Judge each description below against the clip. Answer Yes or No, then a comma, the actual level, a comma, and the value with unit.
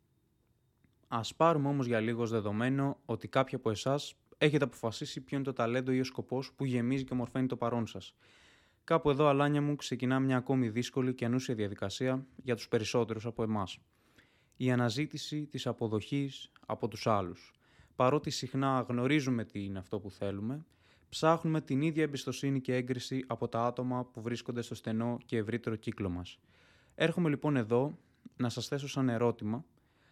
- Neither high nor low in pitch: No, low, 125 Hz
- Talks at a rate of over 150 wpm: Yes, average, 165 wpm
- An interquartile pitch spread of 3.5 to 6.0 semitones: No, average, 2.9 semitones